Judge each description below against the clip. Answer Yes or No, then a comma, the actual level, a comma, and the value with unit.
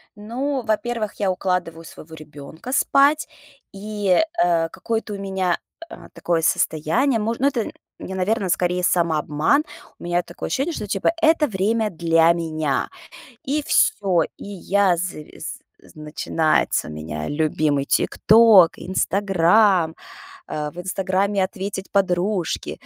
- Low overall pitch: No, medium, 185 Hz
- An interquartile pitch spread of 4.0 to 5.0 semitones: Yes, average, 4.6 semitones